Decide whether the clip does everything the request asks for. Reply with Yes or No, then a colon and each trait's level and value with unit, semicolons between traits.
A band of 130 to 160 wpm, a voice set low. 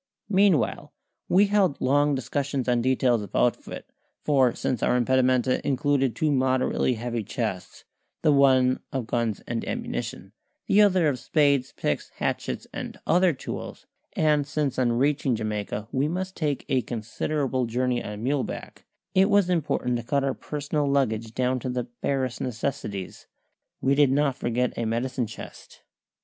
Yes: average, 150 wpm; low, 130 Hz